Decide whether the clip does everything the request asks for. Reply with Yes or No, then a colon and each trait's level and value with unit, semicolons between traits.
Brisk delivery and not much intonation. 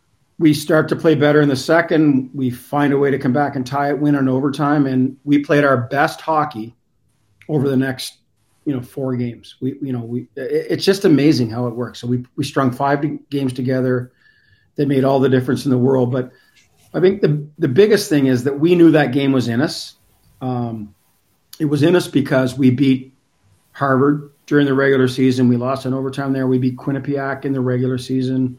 Yes: fast, 210 wpm; narrow, 2.3 semitones